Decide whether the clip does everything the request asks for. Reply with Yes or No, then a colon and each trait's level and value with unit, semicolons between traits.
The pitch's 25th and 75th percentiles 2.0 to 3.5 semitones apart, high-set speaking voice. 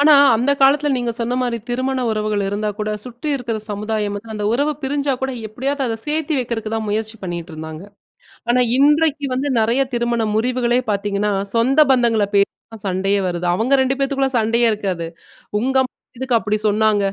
No: average, 4.0 semitones; high, 235 Hz